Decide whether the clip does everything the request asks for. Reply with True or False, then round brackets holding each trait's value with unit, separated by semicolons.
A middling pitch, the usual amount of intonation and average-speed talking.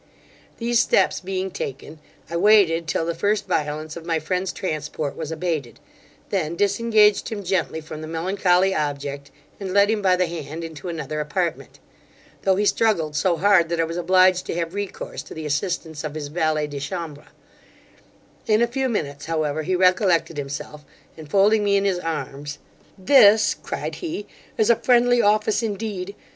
True (175 Hz; 4.6 semitones; 170 wpm)